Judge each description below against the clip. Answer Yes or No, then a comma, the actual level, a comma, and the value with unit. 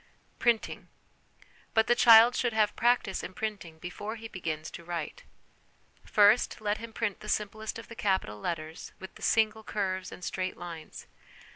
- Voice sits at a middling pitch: No, high, 205 Hz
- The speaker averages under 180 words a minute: Yes, average, 155 wpm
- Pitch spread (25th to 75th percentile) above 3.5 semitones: Yes, average, 3.9 semitones